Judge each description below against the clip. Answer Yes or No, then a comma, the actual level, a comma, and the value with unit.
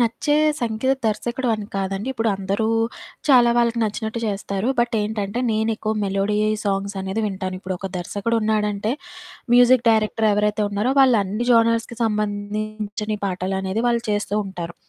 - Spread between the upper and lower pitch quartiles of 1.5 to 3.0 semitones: Yes, narrow, 2.5 semitones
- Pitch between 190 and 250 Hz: Yes, high, 215 Hz